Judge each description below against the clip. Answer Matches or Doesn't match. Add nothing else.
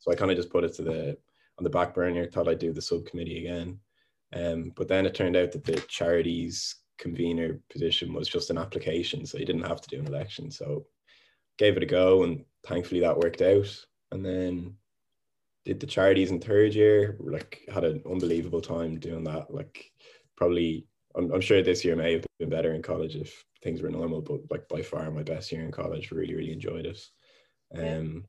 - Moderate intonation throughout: Doesn't match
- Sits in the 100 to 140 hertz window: Doesn't match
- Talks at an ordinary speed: Doesn't match